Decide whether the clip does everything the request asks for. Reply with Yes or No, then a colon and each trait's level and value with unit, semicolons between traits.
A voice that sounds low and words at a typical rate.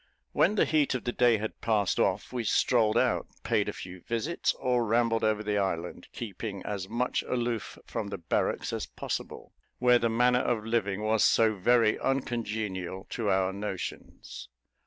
Yes: low, 110 Hz; average, 170 wpm